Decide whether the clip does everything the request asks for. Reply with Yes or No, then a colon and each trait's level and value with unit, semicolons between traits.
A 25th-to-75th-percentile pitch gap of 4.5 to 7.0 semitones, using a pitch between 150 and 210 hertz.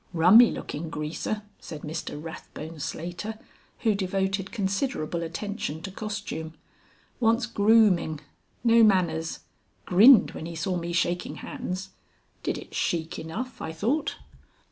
Yes: average, 4.9 semitones; medium, 185 Hz